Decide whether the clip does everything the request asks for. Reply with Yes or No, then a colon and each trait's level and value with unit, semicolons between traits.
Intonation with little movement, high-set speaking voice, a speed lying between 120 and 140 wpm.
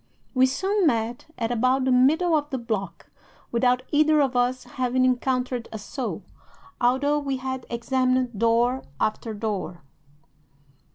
Yes: narrow, 2.0 semitones; very high, 255 Hz; slow, 135 wpm